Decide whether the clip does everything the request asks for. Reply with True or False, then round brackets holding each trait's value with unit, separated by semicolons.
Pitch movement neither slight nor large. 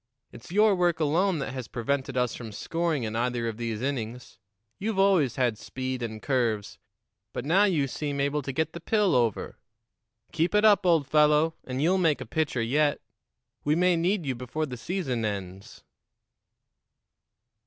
False (5.7 semitones)